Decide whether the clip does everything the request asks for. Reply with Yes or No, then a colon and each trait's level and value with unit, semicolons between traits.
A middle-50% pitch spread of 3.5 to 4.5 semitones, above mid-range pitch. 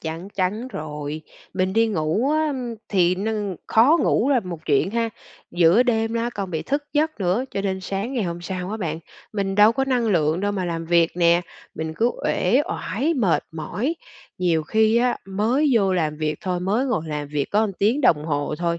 No: wide, 5.4 semitones; high, 195 Hz